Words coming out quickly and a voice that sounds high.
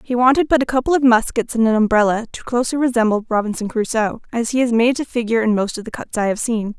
Yes: fast, 255 wpm; high, 230 Hz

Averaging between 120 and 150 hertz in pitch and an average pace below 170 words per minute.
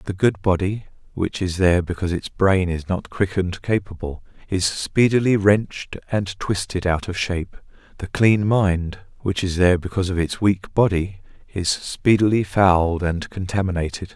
No: very low, 95 Hz; average, 160 wpm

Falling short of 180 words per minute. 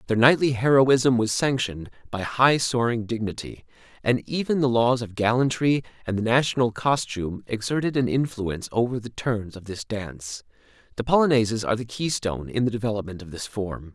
Yes: average, 170 wpm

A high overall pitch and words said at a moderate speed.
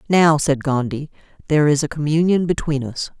No: medium, 150 Hz; average, 170 wpm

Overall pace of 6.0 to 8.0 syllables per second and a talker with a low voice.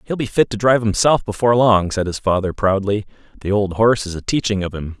Yes: 6.2 syllables/s; low, 105 Hz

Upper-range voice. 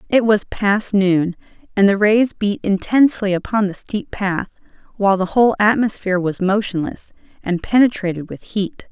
Yes: high, 200 Hz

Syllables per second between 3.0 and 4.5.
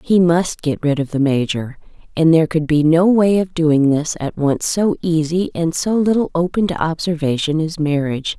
No: 4.9 syllables/s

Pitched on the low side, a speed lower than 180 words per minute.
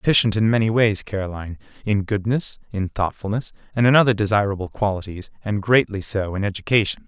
Yes: low, 105 Hz; average, 160 wpm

